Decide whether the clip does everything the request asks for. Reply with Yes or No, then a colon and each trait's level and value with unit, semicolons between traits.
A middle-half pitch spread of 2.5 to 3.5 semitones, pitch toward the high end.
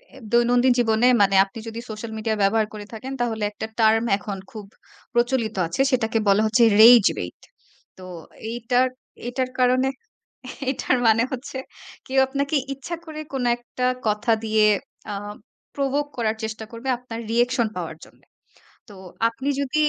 Yes: average, 2.8 semitones; high, 235 Hz